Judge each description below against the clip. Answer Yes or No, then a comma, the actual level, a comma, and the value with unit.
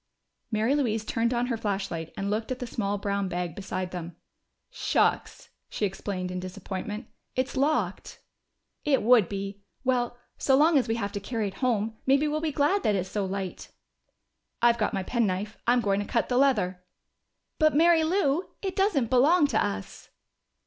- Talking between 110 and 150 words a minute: No, average, 175 wpm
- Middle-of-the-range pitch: No, high, 225 Hz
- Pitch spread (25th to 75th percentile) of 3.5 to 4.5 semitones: No, average, 5.2 semitones